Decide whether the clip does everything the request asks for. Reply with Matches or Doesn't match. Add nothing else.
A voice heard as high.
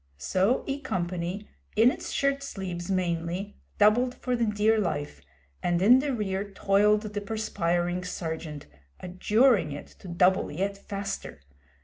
Matches